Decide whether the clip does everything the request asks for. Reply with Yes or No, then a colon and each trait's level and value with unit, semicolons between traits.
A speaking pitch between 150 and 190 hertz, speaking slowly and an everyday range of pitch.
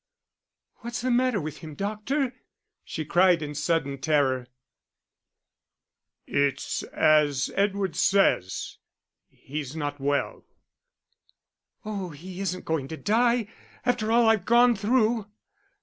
No: medium, 185 Hz; slow, 110 wpm; wide, 7.1 semitones